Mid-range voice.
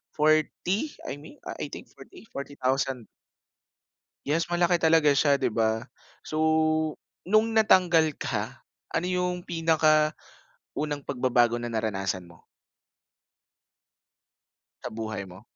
Yes: medium, 150 Hz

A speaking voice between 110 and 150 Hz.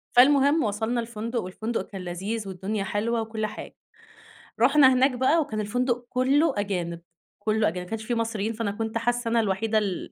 No: high, 225 Hz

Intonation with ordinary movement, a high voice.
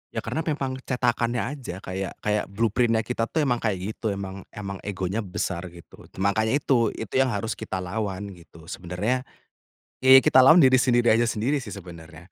No: average, 4.6 semitones; low, 110 Hz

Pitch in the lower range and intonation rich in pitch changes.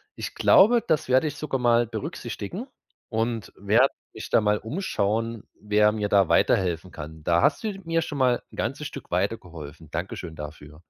Yes: low, 110 Hz; wide, 6.8 semitones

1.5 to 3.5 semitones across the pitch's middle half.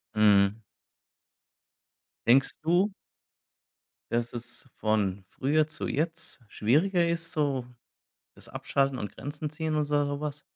No: average, 4.8 semitones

